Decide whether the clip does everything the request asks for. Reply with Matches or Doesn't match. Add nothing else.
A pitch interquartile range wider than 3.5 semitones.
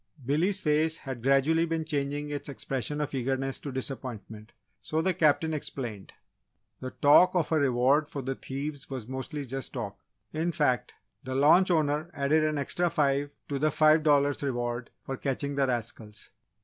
Doesn't match